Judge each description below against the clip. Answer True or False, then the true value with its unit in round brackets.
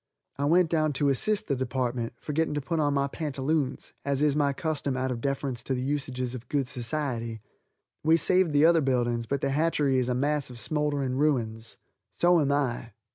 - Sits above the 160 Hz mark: False (140 Hz)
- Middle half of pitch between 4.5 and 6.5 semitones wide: False (2.9 semitones)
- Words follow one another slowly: False (195 wpm)